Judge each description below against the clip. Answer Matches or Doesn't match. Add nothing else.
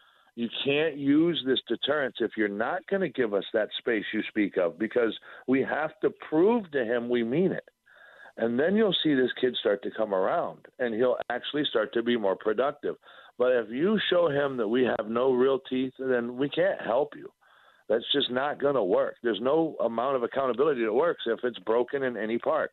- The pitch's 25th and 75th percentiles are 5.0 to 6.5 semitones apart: Matches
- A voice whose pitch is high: Doesn't match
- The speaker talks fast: Matches